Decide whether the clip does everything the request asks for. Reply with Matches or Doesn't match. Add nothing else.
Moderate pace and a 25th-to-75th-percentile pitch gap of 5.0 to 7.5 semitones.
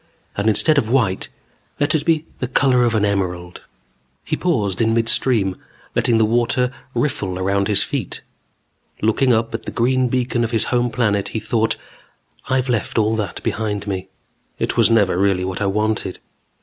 Doesn't match